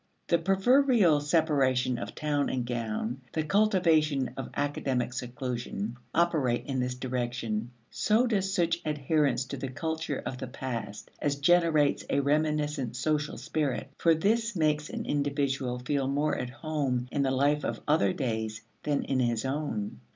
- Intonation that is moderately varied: Yes, average, 3.9 semitones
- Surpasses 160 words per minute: No, average, 150 wpm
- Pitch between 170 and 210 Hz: No, medium, 140 Hz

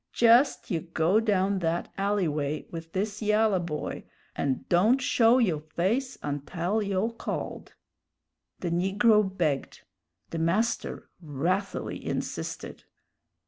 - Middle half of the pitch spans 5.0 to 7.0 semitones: No, average, 4.5 semitones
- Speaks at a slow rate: Yes, slow, 115 wpm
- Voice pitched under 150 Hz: No, high, 190 Hz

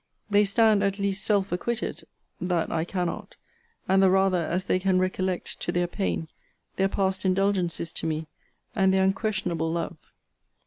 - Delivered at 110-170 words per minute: Yes, average, 160 wpm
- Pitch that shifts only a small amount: Yes, narrow, 2.0 semitones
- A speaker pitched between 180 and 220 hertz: Yes, high, 190 Hz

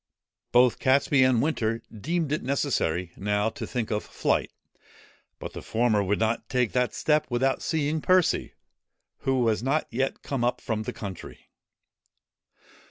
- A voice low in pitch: Yes, low, 125 Hz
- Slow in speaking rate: No, average, 150 wpm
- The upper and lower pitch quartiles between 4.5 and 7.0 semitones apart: No, average, 4.1 semitones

